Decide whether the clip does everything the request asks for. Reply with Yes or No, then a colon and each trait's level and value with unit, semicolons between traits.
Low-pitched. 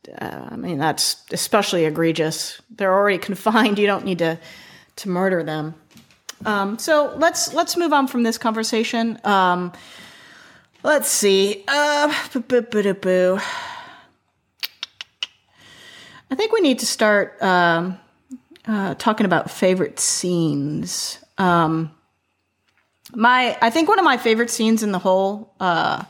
No: high, 205 Hz